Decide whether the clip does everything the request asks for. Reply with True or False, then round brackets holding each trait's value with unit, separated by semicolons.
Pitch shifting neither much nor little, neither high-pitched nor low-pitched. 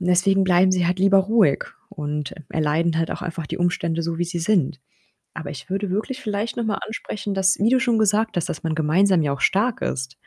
True (3.9 semitones; 180 Hz)